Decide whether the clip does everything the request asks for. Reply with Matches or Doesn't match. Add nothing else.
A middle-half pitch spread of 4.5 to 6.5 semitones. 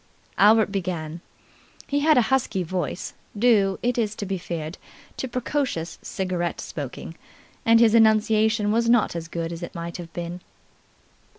Matches